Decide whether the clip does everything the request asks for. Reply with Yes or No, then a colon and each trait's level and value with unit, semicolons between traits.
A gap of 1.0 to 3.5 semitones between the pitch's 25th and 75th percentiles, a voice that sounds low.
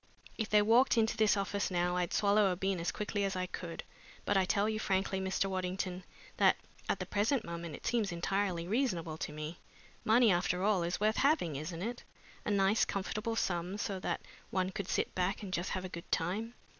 No: average, 3.0 semitones; high, 195 Hz